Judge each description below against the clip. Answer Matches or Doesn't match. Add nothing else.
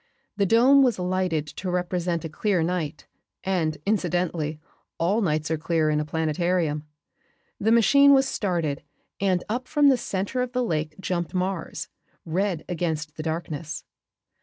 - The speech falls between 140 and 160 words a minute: Matches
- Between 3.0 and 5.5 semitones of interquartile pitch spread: Matches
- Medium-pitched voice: Matches